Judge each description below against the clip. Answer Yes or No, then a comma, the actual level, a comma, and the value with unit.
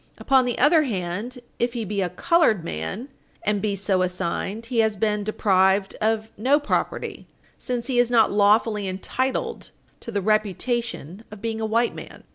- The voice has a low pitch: No, high, 215 Hz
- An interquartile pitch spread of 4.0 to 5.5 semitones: No, average, 3.5 semitones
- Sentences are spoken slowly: No, average, 170 wpm